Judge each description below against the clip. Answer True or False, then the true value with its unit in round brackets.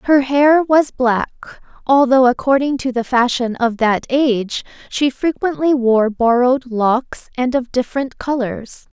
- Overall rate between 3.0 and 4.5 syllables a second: True (4.1 syllables/s)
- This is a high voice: True (255 Hz)